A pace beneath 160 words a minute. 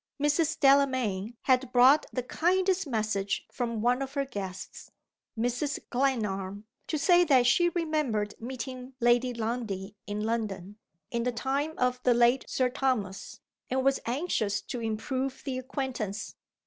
Yes: average, 140 wpm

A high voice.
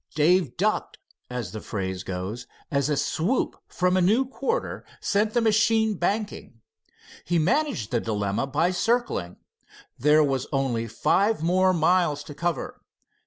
No: medium, 165 Hz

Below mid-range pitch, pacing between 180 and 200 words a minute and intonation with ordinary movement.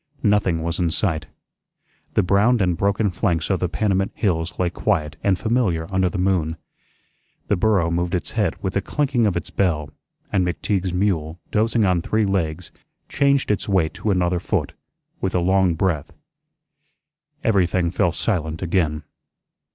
No: very low, 90 Hz; average, 160 wpm; average, 3.2 semitones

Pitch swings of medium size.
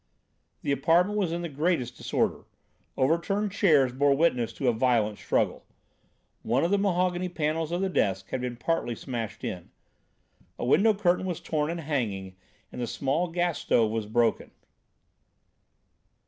No: wide, 6.4 semitones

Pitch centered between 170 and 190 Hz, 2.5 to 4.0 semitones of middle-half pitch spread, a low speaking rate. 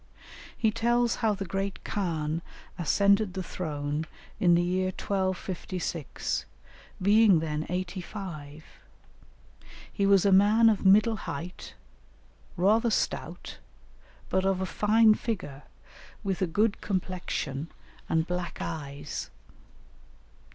Yes: medium, 185 Hz; average, 3.6 semitones; slow, 110 wpm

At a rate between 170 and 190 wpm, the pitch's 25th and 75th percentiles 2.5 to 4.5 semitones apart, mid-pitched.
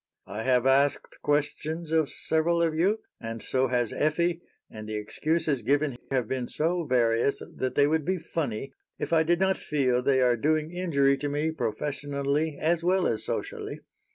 Yes: average, 175 wpm; average, 3.9 semitones; medium, 145 Hz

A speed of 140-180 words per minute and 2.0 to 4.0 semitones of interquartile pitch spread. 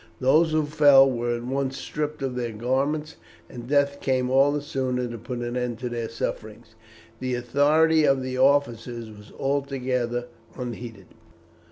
Yes: average, 160 wpm; average, 2.9 semitones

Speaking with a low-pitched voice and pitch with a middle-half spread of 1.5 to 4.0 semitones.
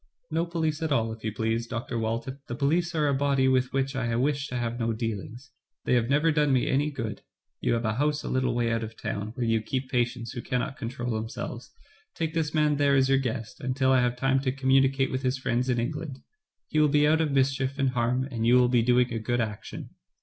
Yes: low, 130 Hz; average, 3.1 semitones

